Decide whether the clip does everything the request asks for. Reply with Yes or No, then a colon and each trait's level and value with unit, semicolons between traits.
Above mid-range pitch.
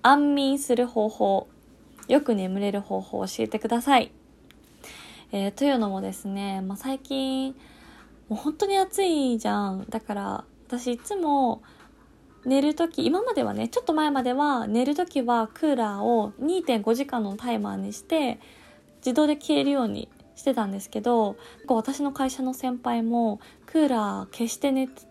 Yes: very high, 250 Hz